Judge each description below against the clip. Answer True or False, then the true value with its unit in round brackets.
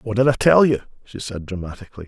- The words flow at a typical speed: False (230 wpm)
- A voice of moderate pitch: False (115 Hz)